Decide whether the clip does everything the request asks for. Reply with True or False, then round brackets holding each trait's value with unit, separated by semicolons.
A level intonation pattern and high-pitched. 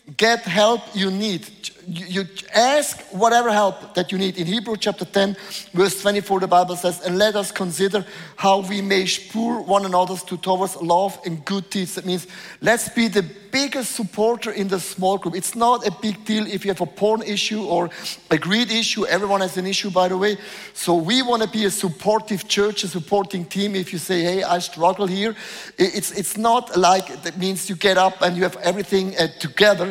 True (2.3 semitones; 195 Hz)